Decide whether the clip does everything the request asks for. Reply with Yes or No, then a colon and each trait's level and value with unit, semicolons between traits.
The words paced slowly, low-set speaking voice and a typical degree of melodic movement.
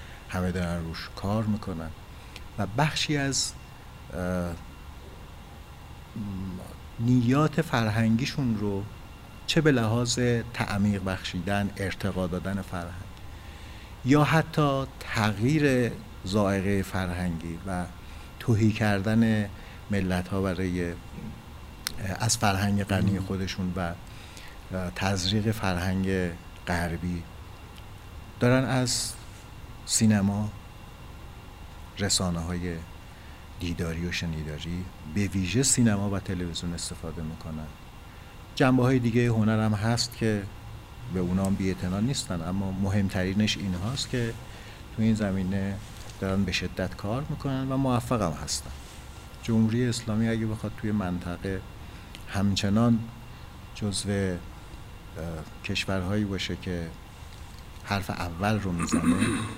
Yes: slow, 95 wpm; very low, 95 Hz; average, 3.8 semitones